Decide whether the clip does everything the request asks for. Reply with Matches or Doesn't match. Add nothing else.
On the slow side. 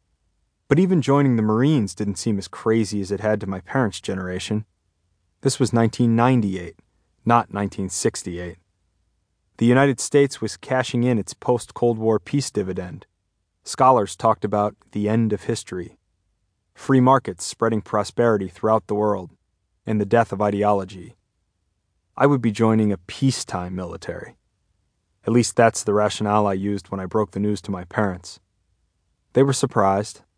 Doesn't match